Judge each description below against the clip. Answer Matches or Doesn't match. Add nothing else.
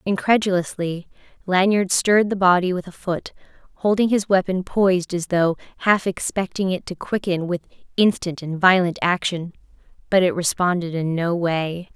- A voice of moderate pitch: Matches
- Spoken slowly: Doesn't match